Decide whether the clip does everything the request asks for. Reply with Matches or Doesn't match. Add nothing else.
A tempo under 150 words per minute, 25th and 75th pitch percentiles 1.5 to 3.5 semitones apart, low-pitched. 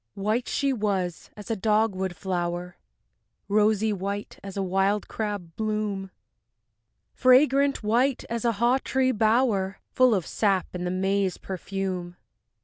Doesn't match